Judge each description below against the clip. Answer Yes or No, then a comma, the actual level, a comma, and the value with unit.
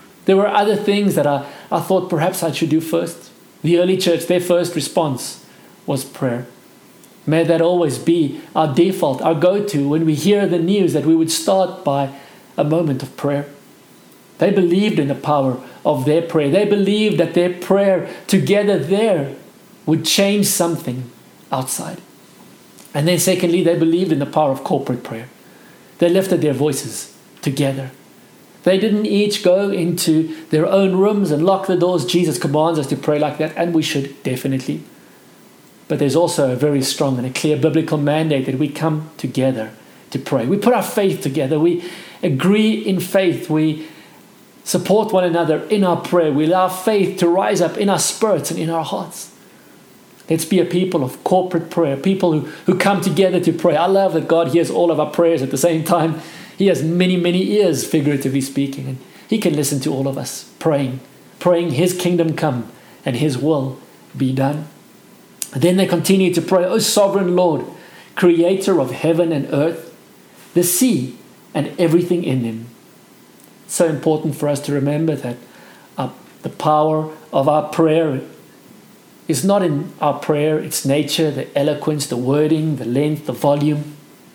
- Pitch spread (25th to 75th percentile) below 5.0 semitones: Yes, average, 3.7 semitones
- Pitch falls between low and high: Yes, medium, 165 Hz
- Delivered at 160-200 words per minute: Yes, average, 175 wpm